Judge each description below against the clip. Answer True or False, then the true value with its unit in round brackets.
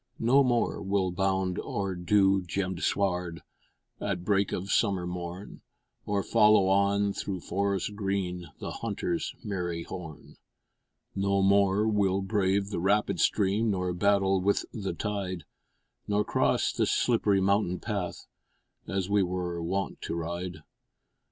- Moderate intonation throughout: False (1.9 semitones)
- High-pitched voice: False (95 Hz)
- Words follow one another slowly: True (130 wpm)